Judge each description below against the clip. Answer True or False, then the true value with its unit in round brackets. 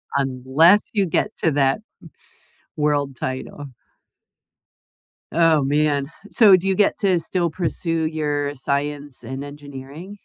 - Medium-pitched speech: True (150 Hz)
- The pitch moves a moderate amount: True (3.3 semitones)